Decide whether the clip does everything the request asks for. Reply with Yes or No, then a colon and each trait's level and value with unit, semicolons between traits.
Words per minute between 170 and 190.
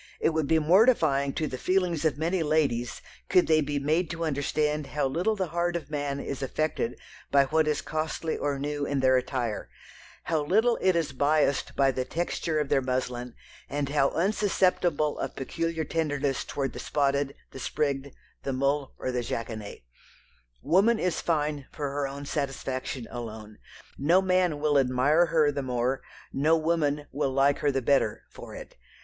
Yes: average, 175 wpm